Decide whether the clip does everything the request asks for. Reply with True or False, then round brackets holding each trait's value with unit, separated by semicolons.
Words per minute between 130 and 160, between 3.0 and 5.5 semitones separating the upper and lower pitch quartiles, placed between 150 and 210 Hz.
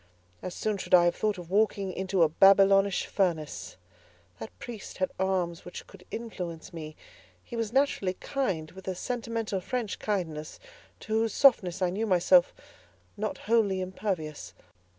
True (150 wpm; 3.6 semitones; 190 Hz)